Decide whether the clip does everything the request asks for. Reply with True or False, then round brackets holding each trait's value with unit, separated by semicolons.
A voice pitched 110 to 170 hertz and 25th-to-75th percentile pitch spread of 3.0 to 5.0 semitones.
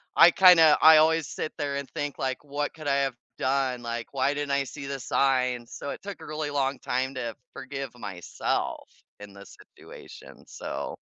False (140 Hz; 2.5 semitones)